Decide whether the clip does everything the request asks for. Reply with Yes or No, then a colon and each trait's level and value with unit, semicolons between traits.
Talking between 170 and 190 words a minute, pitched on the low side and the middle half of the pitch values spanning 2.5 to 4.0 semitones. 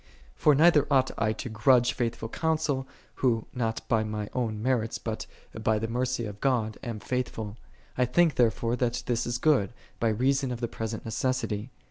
Yes: average, 185 wpm; low, 120 Hz; average, 2.8 semitones